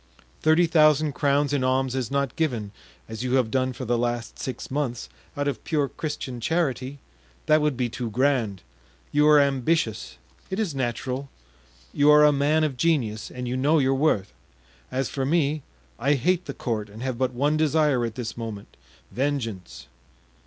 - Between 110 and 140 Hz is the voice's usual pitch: Yes, low, 135 Hz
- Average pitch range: Yes, average, 3.7 semitones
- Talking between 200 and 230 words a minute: No, average, 170 wpm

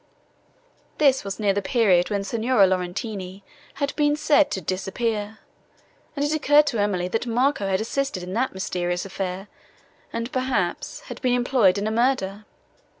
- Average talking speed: Yes, average, 155 wpm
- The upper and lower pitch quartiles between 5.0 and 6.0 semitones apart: Yes, average, 5.3 semitones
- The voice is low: No, high, 215 Hz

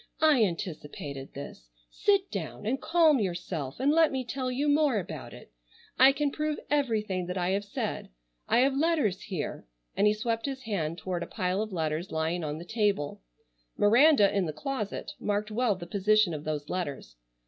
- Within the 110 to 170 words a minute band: No, average, 180 wpm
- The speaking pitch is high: Yes, high, 205 Hz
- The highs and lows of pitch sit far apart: Yes, wide, 7.5 semitones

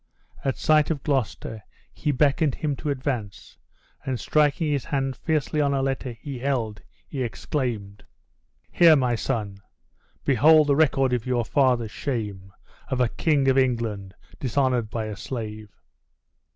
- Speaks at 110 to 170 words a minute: Yes, average, 145 wpm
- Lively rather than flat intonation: No, average, 3.9 semitones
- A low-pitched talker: Yes, low, 130 Hz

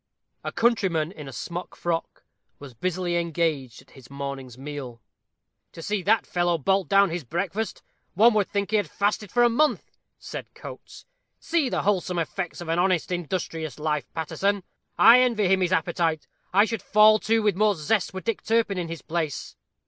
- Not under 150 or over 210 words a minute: Yes, average, 180 wpm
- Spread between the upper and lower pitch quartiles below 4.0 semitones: No, average, 4.5 semitones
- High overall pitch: No, medium, 180 Hz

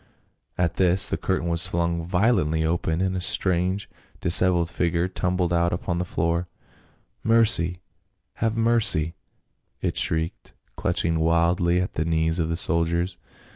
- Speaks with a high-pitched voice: No, very low, 85 Hz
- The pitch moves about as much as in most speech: No, narrow, 1.6 semitones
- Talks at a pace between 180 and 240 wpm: No, average, 145 wpm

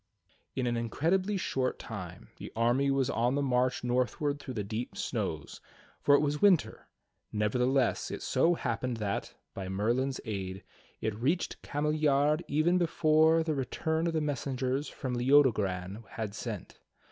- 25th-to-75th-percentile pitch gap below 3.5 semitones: No, average, 4.6 semitones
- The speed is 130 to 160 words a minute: Yes, average, 145 wpm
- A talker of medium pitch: No, low, 130 Hz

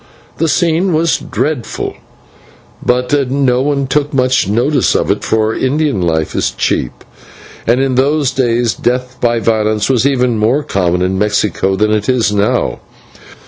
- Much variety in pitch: No, average, 4.4 semitones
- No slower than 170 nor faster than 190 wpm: No, average, 150 wpm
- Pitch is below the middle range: Yes, low, 125 Hz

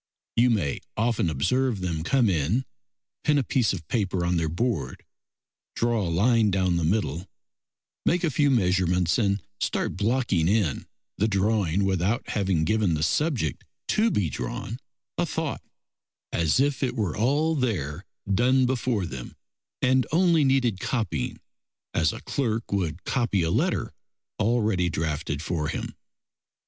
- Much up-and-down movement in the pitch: Yes, wide, 6.3 semitones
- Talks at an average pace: Yes, average, 145 wpm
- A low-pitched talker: Yes, low, 100 Hz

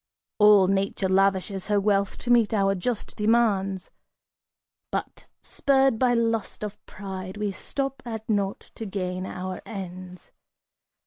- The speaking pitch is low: No, high, 200 Hz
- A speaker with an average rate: No, slow, 130 wpm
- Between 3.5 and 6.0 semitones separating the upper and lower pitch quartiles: No, average, 2.8 semitones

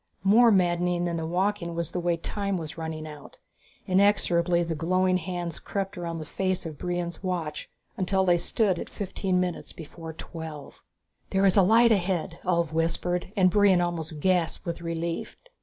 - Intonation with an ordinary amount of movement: No, narrow, 2.1 semitones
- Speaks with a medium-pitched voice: Yes, medium, 175 Hz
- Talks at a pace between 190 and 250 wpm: No, average, 170 wpm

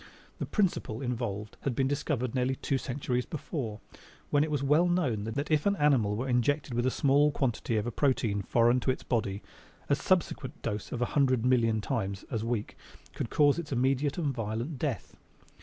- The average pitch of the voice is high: No, low, 130 Hz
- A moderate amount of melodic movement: Yes, average, 3.9 semitones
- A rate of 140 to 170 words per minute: No, average, 185 wpm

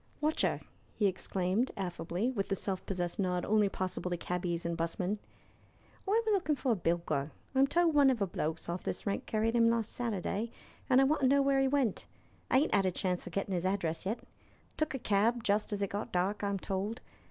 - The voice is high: Yes, high, 200 Hz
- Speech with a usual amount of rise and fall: No, wide, 5.8 semitones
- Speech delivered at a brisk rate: Yes, fast, 215 wpm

